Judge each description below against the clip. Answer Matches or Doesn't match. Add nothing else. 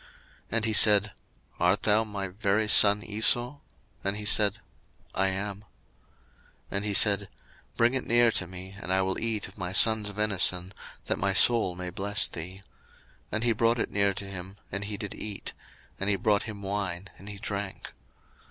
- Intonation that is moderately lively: Doesn't match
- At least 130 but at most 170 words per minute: Doesn't match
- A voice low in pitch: Matches